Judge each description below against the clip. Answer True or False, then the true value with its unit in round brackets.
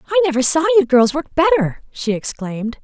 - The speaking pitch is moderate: False (290 Hz)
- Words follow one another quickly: False (190 wpm)